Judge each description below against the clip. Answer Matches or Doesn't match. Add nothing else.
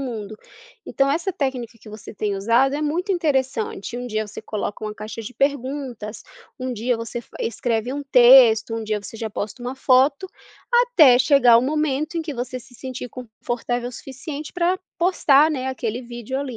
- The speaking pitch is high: Matches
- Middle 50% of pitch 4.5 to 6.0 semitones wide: Doesn't match